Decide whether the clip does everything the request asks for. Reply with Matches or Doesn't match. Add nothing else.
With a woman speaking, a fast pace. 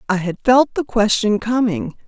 Doesn't match